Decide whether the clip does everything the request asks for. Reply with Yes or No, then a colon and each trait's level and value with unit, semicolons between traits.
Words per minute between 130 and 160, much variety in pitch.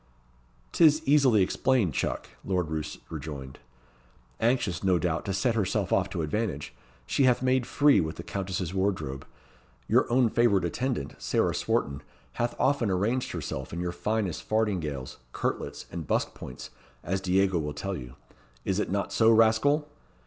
Yes: average, 155 wpm; wide, 6.3 semitones